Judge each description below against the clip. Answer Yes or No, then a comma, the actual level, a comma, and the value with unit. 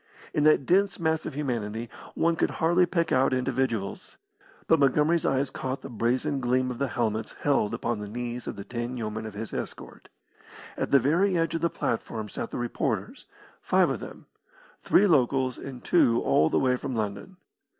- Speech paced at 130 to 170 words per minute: No, average, 185 wpm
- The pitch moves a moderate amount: Yes, average, 4.8 semitones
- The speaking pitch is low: Yes, low, 130 Hz